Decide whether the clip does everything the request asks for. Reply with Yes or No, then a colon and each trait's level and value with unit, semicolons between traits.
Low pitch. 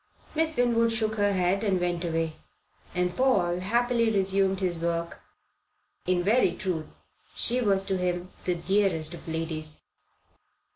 No: medium, 185 Hz